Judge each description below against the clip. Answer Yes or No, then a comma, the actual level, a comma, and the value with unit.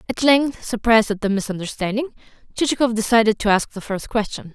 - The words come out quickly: No, average, 170 wpm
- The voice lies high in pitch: Yes, high, 225 Hz